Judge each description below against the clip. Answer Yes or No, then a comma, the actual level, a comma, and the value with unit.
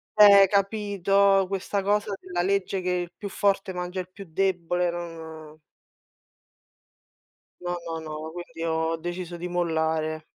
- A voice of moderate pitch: Yes, medium, 180 Hz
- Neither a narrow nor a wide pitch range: Yes, average, 3.0 semitones